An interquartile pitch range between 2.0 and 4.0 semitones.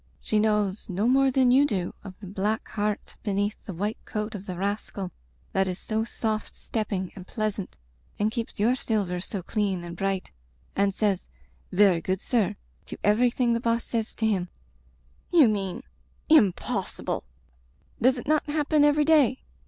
Yes: average, 3.5 semitones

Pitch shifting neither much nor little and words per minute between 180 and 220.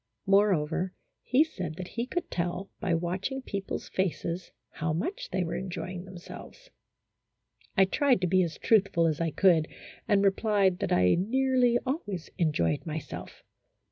No: average, 3.7 semitones; average, 145 wpm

